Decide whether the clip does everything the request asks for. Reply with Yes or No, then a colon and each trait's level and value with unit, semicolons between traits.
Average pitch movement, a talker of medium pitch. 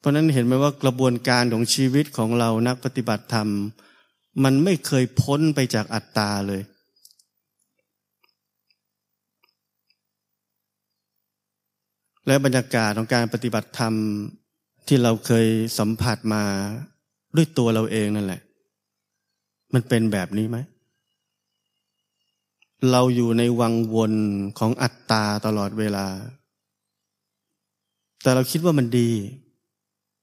No: average, 3.6 semitones; low, 115 Hz